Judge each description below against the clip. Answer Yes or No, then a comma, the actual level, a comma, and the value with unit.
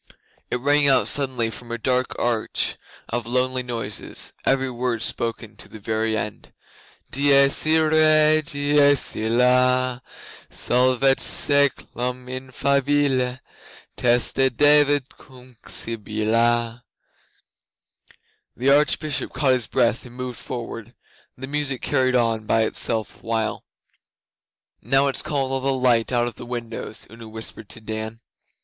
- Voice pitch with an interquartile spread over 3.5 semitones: No, average, 2.9 semitones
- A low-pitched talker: Yes, low, 125 Hz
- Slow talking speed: Yes, slow, 125 wpm